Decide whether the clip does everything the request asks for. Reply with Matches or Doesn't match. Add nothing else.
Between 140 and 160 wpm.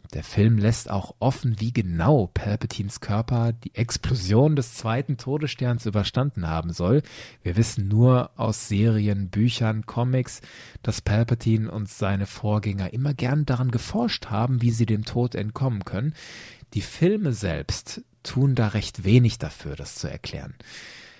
Matches